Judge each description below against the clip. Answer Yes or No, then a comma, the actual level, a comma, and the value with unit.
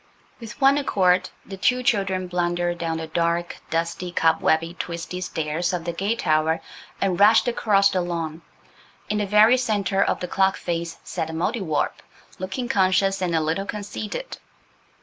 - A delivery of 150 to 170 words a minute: Yes, average, 160 wpm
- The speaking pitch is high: No, medium, 180 Hz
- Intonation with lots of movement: No, average, 3.3 semitones